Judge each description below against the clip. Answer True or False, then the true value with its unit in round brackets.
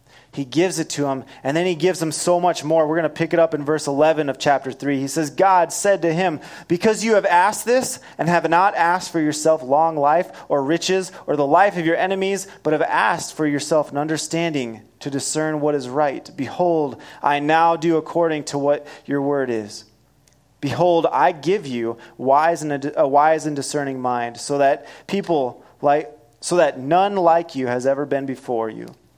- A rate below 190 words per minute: False (200 wpm)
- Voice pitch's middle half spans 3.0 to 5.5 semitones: True (3.4 semitones)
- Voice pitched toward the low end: False (155 Hz)